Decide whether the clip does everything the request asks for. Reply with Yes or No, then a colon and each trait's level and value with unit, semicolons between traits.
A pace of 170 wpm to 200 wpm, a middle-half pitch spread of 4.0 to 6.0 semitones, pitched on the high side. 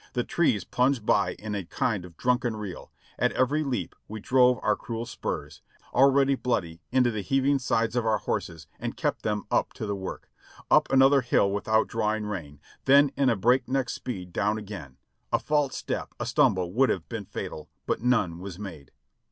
No: average, 185 wpm; average, 4.6 semitones; low, 110 Hz